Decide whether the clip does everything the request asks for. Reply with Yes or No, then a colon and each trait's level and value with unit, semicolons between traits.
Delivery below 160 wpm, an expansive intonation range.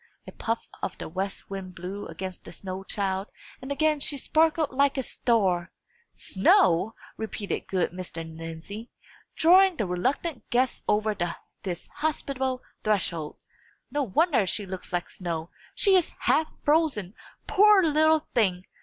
Yes: average, 140 wpm; wide, 7.9 semitones